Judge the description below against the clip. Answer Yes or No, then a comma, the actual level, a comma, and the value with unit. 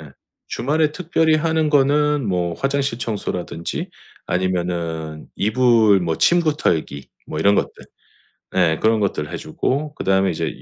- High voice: No, low, 105 Hz